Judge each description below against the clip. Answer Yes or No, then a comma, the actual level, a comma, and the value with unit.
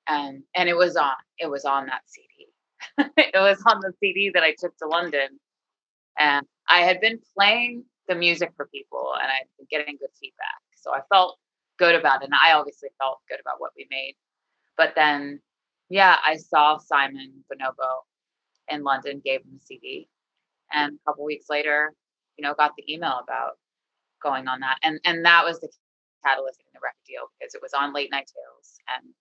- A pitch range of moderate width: No, wide, 5.7 semitones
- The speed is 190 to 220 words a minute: Yes, average, 195 wpm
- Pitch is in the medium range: Yes, medium, 150 Hz